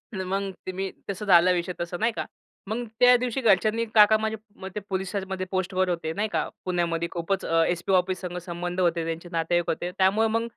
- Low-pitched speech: No, medium, 185 Hz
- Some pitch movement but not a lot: Yes, average, 3.0 semitones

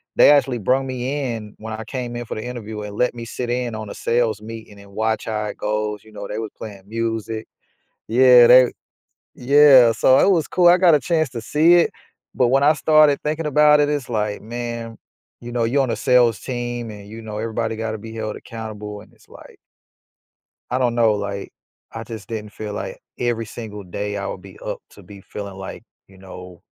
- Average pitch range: Yes, average, 3.0 semitones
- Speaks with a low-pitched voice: Yes, low, 115 Hz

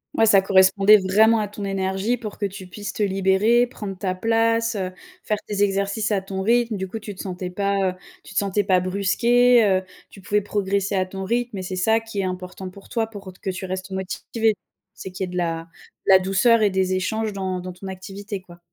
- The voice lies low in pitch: No, high, 195 Hz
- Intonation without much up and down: Yes, narrow, 2.3 semitones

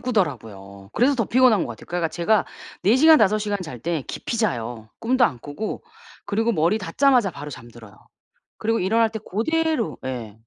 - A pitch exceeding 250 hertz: No, high, 195 Hz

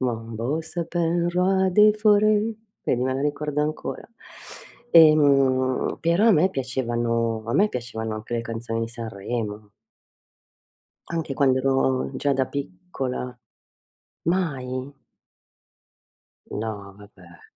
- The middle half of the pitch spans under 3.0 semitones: No, wide, 6.0 semitones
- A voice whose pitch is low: Yes, low, 130 Hz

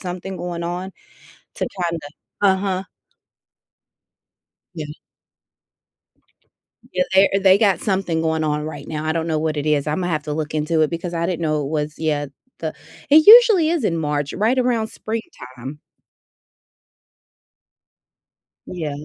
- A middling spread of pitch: Yes, average, 3.9 semitones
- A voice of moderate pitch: Yes, medium, 165 Hz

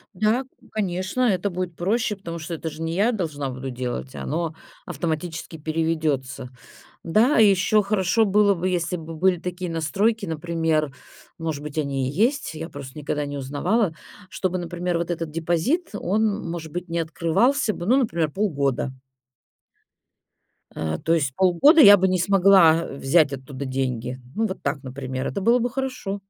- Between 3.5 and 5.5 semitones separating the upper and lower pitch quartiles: Yes, average, 4.9 semitones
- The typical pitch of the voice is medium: Yes, medium, 170 Hz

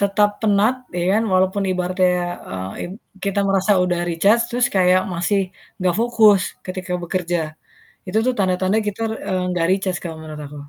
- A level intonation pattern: Yes, narrow, 2.3 semitones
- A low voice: No, medium, 185 Hz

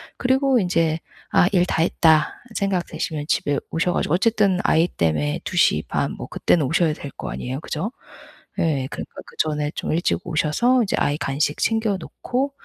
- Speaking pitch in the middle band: Yes, medium, 165 Hz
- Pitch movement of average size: Yes, average, 4.8 semitones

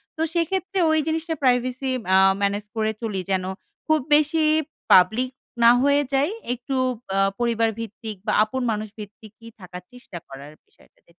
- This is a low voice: No, high, 230 Hz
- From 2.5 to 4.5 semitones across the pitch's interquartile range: No, average, 5.2 semitones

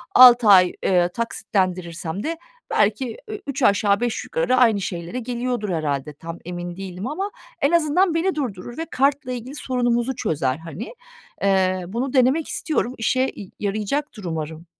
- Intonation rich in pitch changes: Yes, wide, 6.2 semitones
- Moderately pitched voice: No, high, 225 Hz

